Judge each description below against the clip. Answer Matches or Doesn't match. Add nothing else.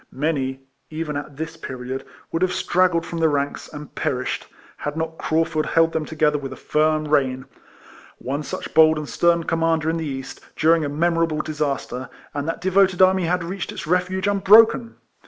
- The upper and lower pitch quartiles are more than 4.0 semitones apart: Doesn't match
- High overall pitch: Doesn't match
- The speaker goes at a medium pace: Matches